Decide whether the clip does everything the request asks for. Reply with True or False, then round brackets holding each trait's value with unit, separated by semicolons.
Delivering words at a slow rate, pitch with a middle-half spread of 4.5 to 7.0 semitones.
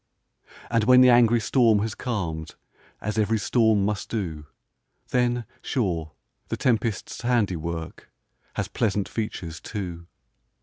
True (120 wpm; 5.3 semitones)